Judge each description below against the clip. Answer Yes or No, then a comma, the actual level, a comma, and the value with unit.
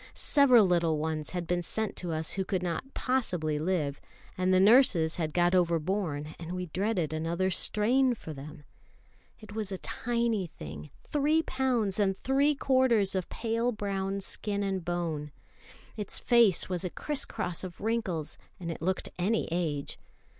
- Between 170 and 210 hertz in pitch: Yes, medium, 185 Hz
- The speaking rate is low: No, average, 160 wpm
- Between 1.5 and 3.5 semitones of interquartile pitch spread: No, average, 5.1 semitones